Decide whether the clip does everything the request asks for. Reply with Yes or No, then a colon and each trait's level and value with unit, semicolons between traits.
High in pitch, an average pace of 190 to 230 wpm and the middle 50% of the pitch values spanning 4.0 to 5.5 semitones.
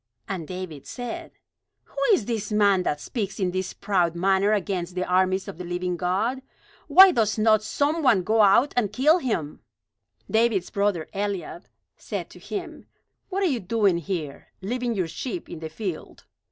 No: high, 200 Hz; average, 170 wpm; average, 4.3 semitones